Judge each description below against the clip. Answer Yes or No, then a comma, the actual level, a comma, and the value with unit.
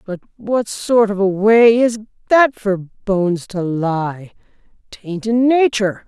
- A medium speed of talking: Yes, average, 150 wpm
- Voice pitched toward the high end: Yes, high, 210 Hz